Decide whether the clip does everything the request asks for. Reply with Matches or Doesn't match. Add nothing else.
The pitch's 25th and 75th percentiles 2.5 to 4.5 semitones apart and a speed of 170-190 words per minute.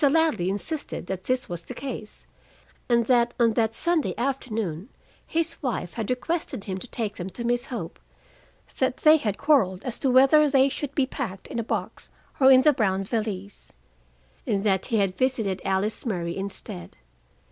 Doesn't match